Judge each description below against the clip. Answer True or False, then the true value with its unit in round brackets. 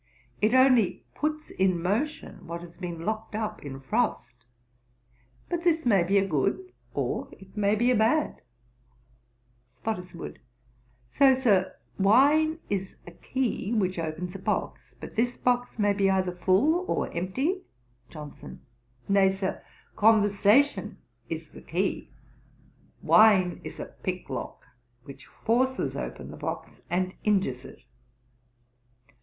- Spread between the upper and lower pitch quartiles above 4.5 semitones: True (5.2 semitones)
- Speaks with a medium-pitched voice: False (205 Hz)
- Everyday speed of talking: False (125 wpm)